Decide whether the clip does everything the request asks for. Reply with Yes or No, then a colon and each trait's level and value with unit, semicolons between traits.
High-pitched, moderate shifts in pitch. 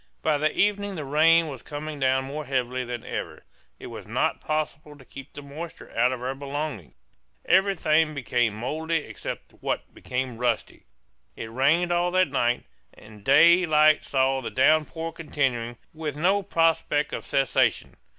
No: medium, 145 Hz; average, 3.9 semitones